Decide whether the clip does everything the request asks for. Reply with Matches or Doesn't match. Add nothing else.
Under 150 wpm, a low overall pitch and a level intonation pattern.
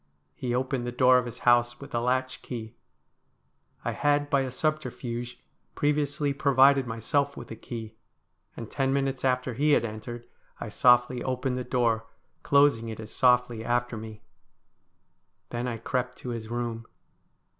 Doesn't match